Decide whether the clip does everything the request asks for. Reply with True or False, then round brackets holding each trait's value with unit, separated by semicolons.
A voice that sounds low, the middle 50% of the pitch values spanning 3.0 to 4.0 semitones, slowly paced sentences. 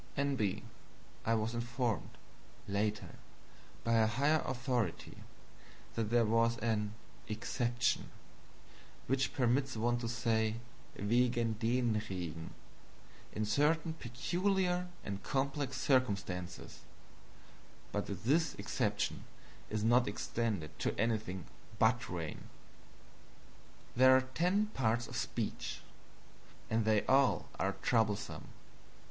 True (115 Hz; 3.3 semitones; 105 wpm)